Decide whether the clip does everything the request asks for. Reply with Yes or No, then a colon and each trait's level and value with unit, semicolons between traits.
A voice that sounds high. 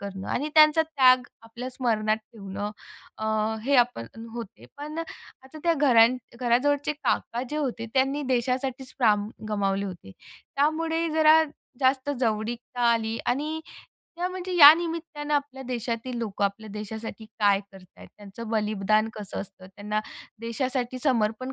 Yes: high, 240 Hz